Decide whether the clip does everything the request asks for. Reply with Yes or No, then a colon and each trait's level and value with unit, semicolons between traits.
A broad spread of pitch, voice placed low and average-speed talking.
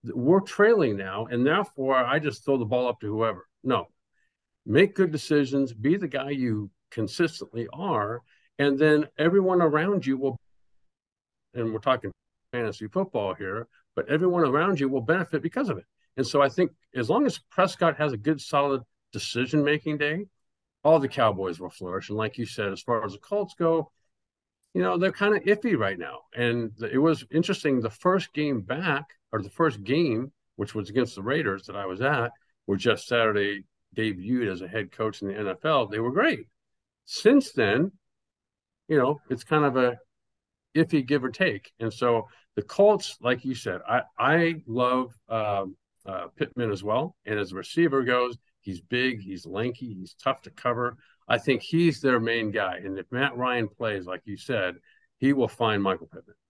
Yes: wide, 5.8 semitones; low, 125 Hz; average, 185 wpm